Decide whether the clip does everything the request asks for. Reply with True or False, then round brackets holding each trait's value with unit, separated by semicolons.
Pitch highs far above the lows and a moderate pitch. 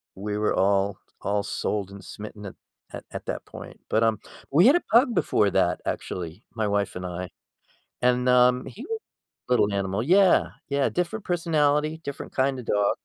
False (6.7 semitones; 115 Hz)